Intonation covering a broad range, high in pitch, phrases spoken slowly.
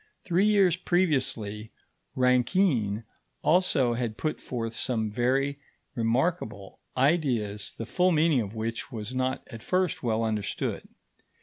No: wide, 6.4 semitones; low, 125 Hz; slow, 120 wpm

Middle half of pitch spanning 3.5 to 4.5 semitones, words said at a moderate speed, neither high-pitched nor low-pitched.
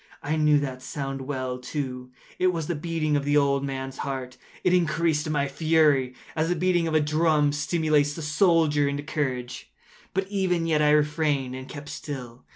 No: average, 2.8 semitones; average, 180 wpm; medium, 150 Hz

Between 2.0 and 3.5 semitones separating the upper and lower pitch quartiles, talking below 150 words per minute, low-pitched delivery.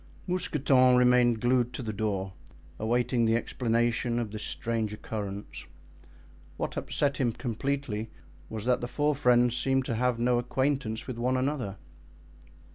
Yes: narrow, 2.4 semitones; average, 140 wpm; low, 120 Hz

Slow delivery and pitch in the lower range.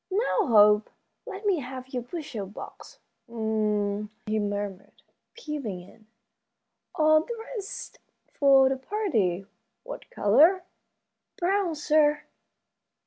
No: slow, 100 wpm; very high, 265 Hz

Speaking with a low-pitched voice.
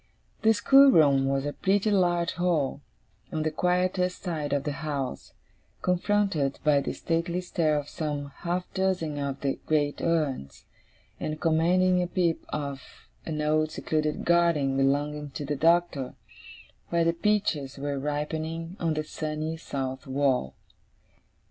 No: medium, 155 Hz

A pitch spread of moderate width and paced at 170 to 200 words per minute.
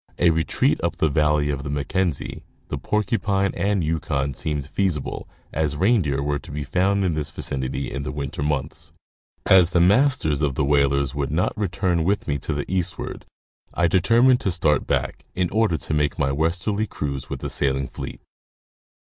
Yes: average, 4.8 semitones; average, 180 wpm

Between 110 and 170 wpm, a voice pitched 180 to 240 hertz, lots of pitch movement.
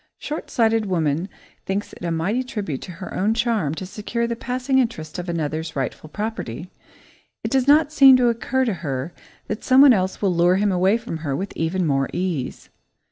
No: average, 190 wpm; high, 190 Hz; wide, 6.2 semitones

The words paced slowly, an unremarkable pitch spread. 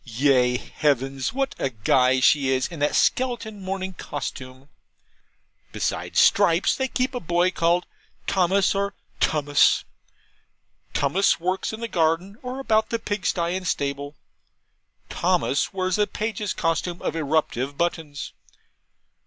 No: slow, 130 wpm; wide, 5.8 semitones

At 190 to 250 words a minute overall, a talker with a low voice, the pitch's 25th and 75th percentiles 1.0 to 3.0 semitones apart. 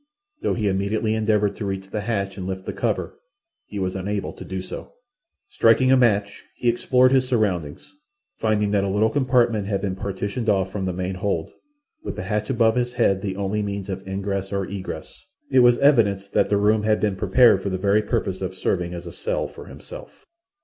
Yes: fast, 205 wpm; low, 100 Hz; narrow, 2.6 semitones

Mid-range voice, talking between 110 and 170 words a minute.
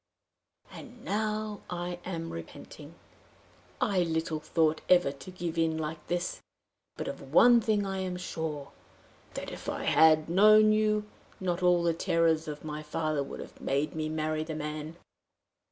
Yes: medium, 165 Hz; average, 155 wpm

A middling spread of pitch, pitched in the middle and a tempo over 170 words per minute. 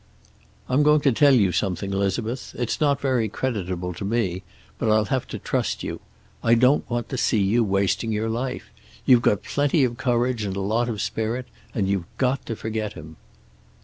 No: average, 4.3 semitones; low, 115 Hz; average, 190 wpm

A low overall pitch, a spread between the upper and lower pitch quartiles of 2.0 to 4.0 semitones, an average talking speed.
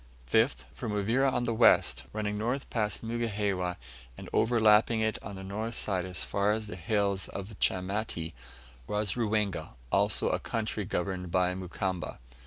Yes: low, 105 Hz; average, 2.7 semitones; average, 155 wpm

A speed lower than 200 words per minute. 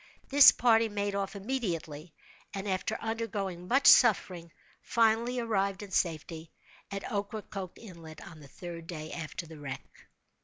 Yes: average, 140 wpm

